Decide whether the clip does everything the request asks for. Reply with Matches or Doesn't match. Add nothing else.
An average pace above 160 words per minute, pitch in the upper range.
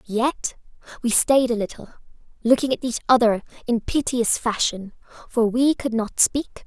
Doesn't match